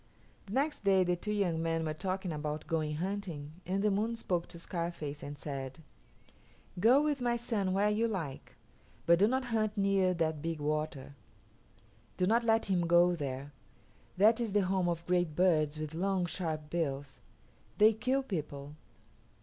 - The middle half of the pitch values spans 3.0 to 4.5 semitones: No, average, 4.9 semitones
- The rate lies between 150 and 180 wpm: Yes, average, 170 wpm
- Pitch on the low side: No, medium, 180 Hz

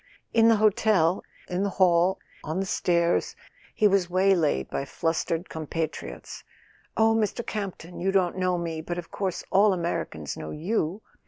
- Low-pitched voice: No, medium, 180 Hz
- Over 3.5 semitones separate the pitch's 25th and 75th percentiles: No, average, 3.1 semitones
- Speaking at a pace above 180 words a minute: No, average, 160 wpm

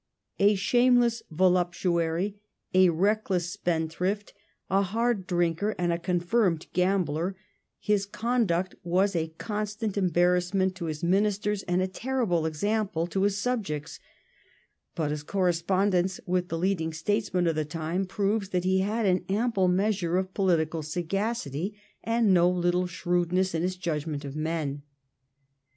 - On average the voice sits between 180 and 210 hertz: Yes, medium, 185 Hz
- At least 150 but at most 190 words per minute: No, average, 140 wpm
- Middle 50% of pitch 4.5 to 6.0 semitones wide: No, average, 3.0 semitones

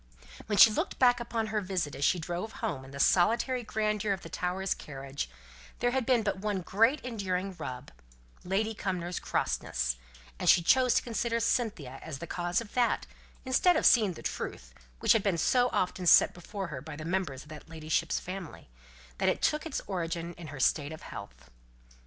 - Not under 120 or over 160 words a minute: No, average, 195 wpm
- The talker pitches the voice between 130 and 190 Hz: Yes, medium, 185 Hz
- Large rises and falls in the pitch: Yes, wide, 5.9 semitones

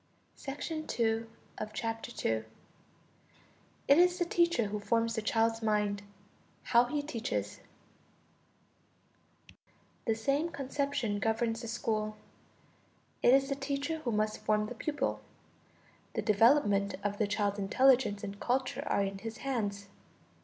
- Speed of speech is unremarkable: No, slow, 115 wpm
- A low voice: No, high, 230 Hz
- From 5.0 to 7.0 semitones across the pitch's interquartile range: No, average, 4.4 semitones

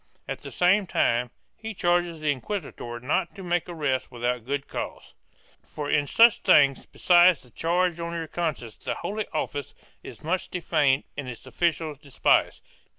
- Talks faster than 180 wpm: No, average, 160 wpm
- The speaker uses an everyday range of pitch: Yes, average, 4.5 semitones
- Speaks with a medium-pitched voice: Yes, medium, 160 Hz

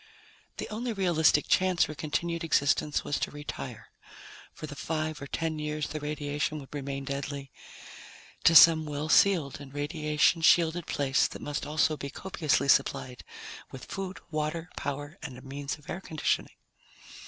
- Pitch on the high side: No, medium, 150 Hz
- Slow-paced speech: No, average, 155 wpm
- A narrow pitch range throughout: Yes, narrow, 2.3 semitones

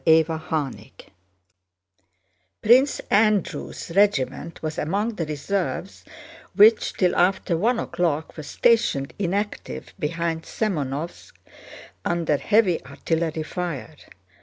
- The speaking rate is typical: No, slow, 95 wpm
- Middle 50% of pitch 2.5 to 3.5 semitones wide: No, average, 4.6 semitones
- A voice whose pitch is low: No, medium, 170 Hz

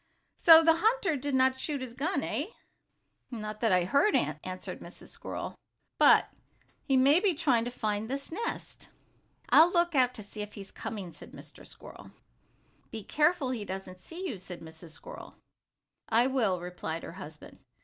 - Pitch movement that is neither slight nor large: No, wide, 7.9 semitones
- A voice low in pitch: No, high, 245 Hz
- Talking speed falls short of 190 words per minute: Yes, average, 170 wpm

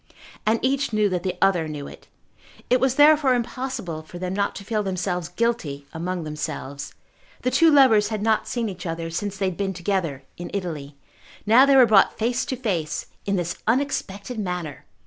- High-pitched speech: Yes, high, 195 Hz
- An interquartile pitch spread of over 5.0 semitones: Yes, wide, 5.5 semitones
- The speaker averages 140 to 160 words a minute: No, average, 185 wpm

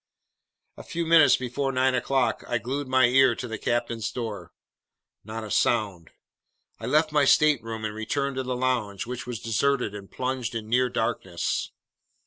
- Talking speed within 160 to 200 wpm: Yes, average, 165 wpm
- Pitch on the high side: No, low, 125 Hz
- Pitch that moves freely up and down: No, average, 2.9 semitones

